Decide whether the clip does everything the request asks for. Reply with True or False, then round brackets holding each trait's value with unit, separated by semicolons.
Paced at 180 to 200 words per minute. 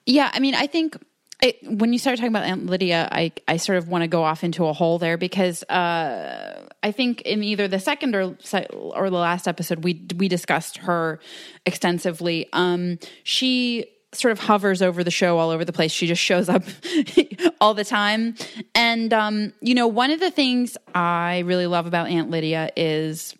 True (195 wpm)